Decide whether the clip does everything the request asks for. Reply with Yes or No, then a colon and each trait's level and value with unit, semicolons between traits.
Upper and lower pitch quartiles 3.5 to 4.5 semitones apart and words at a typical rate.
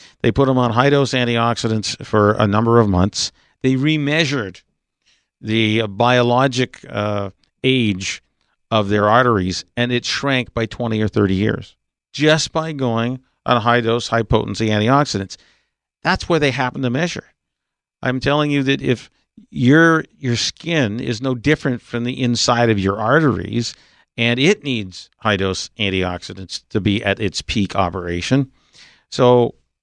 Yes: average, 4.0 semitones; average, 150 wpm